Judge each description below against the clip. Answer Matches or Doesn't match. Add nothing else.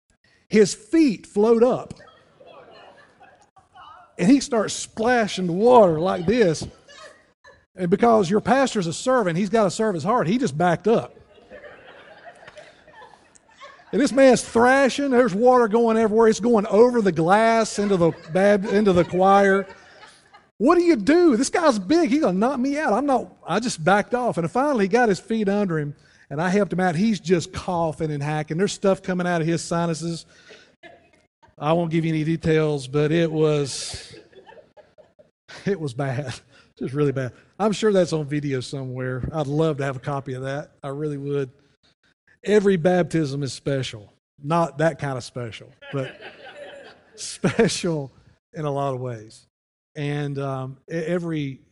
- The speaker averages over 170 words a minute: Doesn't match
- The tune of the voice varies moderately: Doesn't match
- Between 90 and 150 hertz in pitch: Doesn't match